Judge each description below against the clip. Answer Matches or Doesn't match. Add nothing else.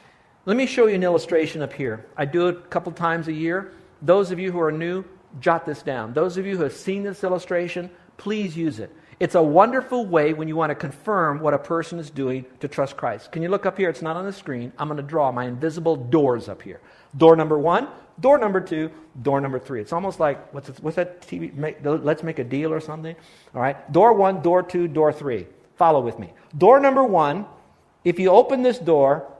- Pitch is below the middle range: Doesn't match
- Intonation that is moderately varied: Matches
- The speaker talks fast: Matches